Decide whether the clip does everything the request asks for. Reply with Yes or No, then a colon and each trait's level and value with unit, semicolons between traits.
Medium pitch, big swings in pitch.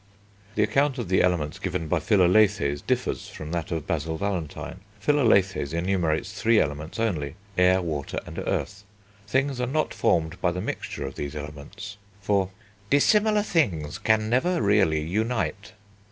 No: very low, 95 Hz; wide, 5.8 semitones